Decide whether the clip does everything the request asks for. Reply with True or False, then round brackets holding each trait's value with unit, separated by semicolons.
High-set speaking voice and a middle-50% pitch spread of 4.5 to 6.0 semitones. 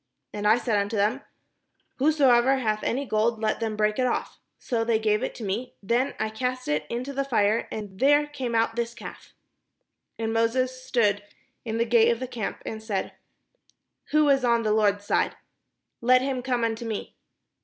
False (230 Hz; 2.9 semitones)